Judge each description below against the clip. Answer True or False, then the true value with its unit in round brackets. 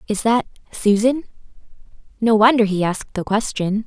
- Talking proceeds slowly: True (125 wpm)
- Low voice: False (215 Hz)